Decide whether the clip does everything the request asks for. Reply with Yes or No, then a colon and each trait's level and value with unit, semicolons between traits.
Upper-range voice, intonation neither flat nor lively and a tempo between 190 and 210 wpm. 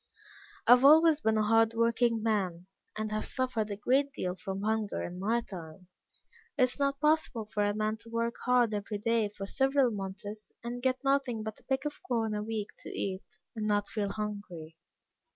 Yes: high, 220 Hz; average, 3.2 semitones; average, 195 wpm